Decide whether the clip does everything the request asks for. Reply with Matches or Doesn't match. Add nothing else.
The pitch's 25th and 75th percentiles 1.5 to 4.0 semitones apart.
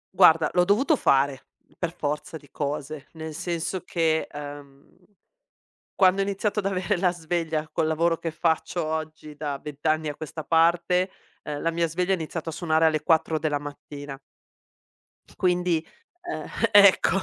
Matches